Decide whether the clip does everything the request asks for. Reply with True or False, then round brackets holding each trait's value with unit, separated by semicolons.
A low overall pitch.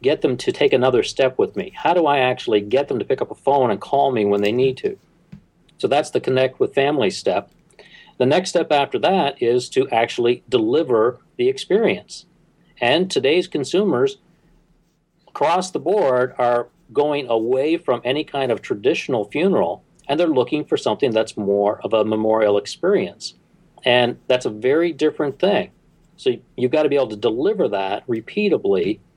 False (145 Hz)